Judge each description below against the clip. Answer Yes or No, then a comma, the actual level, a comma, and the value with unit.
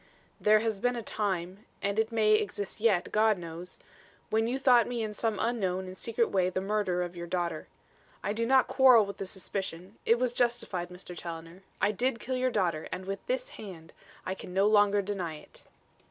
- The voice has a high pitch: Yes, high, 205 Hz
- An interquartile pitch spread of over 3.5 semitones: Yes, average, 4.0 semitones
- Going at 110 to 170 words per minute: No, average, 200 wpm